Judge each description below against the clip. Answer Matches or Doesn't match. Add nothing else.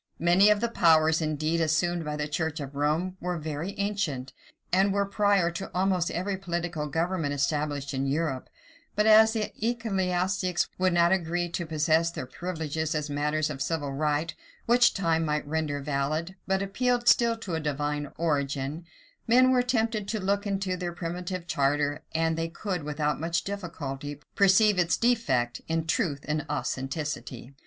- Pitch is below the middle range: Doesn't match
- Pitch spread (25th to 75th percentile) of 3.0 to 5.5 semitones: Matches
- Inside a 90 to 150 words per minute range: Doesn't match